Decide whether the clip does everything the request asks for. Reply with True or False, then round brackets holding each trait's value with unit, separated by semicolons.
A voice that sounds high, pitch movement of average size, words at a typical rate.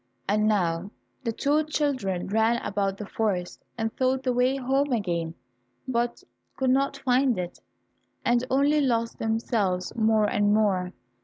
True (225 Hz; 4.5 semitones; 145 wpm)